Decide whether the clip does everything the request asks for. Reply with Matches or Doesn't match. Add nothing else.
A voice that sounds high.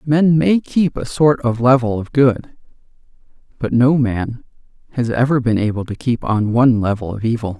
Doesn't match